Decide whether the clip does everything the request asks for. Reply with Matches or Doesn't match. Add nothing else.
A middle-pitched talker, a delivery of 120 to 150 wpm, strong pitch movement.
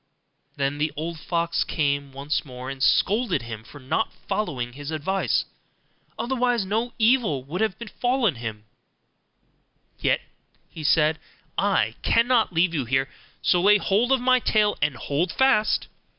Matches